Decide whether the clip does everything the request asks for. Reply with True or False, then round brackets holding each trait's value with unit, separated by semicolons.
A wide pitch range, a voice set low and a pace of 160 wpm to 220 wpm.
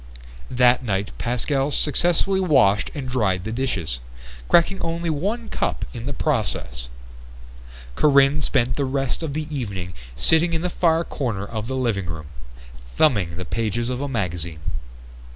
False (7.1 semitones; 125 Hz; 150 wpm)